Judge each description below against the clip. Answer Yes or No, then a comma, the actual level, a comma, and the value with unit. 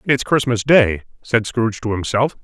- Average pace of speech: Yes, average, 170 wpm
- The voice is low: Yes, low, 120 Hz